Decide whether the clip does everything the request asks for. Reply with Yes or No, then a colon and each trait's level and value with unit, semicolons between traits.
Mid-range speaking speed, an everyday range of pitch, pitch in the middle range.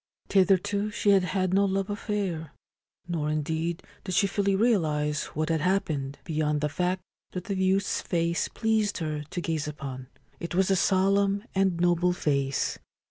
Yes: average, 160 wpm; average, 4.0 semitones; medium, 180 Hz